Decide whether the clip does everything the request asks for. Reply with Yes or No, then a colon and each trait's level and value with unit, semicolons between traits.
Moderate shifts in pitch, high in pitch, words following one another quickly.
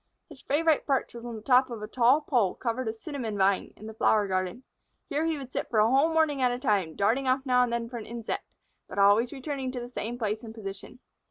Yes: average, 3.6 semitones; high, 240 Hz; fast, 250 wpm